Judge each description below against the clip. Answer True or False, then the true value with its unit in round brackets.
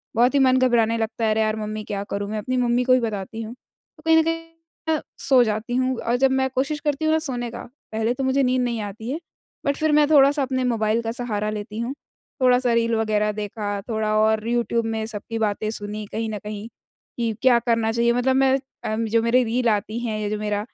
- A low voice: False (230 Hz)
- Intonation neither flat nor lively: True (3.1 semitones)